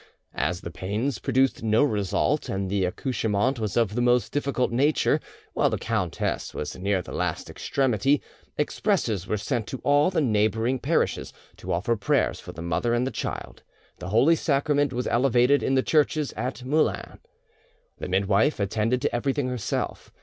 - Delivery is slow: No, average, 165 wpm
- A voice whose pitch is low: Yes, low, 120 Hz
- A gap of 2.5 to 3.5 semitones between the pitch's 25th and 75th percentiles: No, average, 4.9 semitones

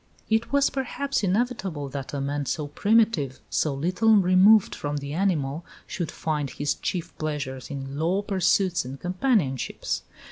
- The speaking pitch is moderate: Yes, medium, 170 Hz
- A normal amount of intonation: No, wide, 6.1 semitones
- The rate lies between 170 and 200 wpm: No, average, 145 wpm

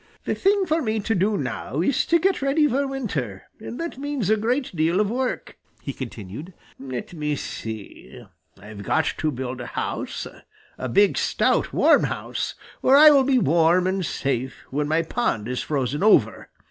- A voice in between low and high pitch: Yes, medium, 180 Hz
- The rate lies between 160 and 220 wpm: Yes, average, 180 wpm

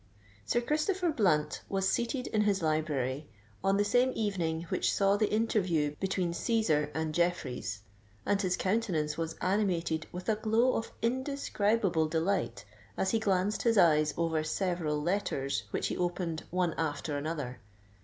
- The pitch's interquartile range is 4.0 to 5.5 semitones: Yes, average, 5.2 semitones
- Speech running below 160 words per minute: Yes, average, 150 wpm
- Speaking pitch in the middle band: Yes, medium, 180 Hz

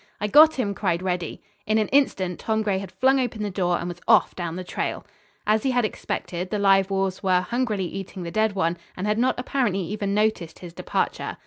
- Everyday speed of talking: No, fast, 220 wpm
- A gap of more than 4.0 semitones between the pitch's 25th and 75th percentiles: No, average, 3.2 semitones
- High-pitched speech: Yes, high, 195 Hz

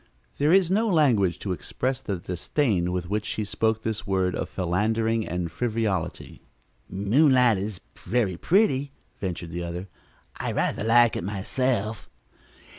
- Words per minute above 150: No, average, 140 wpm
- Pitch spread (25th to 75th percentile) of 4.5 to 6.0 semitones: Yes, average, 5.2 semitones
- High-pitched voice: No, low, 110 Hz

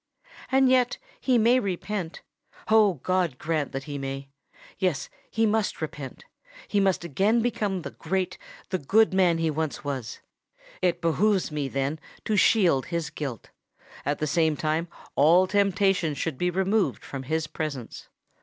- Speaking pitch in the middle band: Yes, medium, 170 Hz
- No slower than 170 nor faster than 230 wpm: No, average, 145 wpm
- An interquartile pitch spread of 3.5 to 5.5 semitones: Yes, average, 5.2 semitones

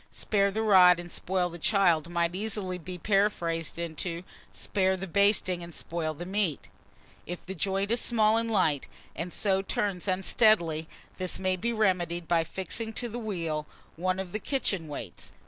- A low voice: No, medium, 185 Hz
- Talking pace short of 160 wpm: No, average, 170 wpm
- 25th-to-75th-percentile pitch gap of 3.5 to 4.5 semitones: No, average, 3.1 semitones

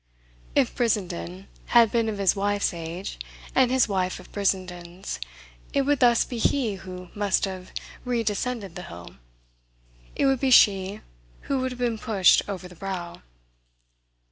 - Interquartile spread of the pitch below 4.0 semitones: No, average, 4.5 semitones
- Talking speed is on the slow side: No, average, 150 wpm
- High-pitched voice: Yes, high, 200 Hz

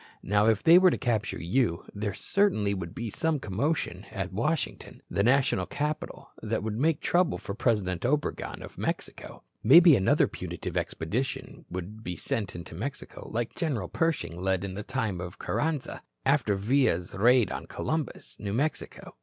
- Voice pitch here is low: Yes, low, 110 Hz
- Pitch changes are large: Yes, wide, 6.8 semitones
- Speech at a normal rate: Yes, average, 160 wpm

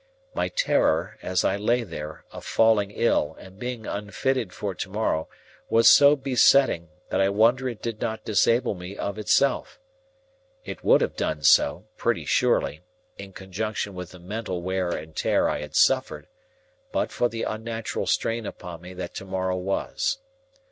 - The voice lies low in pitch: Yes, low, 105 Hz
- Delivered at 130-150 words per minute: No, average, 165 wpm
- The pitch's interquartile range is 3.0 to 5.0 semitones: Yes, average, 4.0 semitones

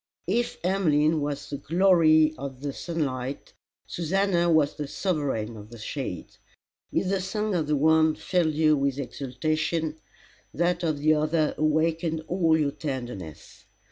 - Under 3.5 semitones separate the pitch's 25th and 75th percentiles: Yes, average, 2.9 semitones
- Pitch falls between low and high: Yes, medium, 155 Hz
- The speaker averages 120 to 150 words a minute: Yes, average, 140 wpm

